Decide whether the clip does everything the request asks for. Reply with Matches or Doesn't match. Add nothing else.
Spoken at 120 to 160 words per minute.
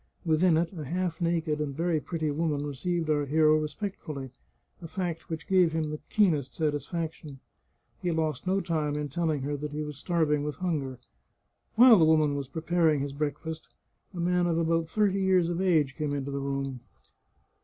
Doesn't match